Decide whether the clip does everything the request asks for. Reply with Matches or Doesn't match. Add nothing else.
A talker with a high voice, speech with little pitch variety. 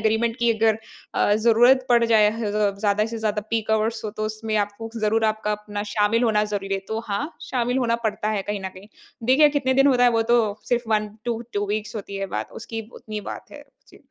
Matches